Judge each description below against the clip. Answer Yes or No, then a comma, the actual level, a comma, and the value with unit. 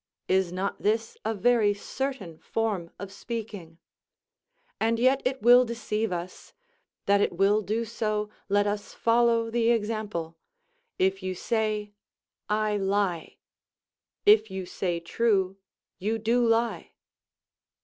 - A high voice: Yes, high, 210 Hz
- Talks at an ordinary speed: No, slow, 125 wpm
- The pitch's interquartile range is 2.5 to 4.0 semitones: Yes, average, 3.0 semitones